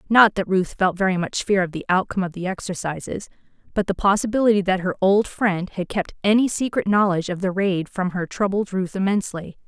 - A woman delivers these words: Yes, female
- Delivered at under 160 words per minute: No, fast, 205 wpm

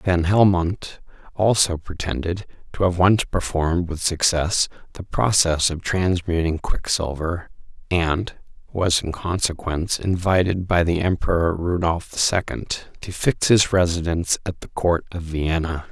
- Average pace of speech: No, slow, 130 wpm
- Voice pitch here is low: Yes, very low, 85 Hz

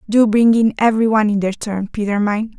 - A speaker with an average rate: No, fast, 230 wpm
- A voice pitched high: Yes, high, 215 Hz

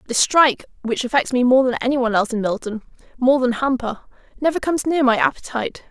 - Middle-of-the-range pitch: No, very high, 260 Hz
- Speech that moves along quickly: No, average, 185 wpm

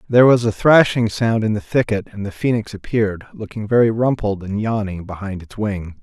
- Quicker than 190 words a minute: Yes, average, 200 wpm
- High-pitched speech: No, low, 105 Hz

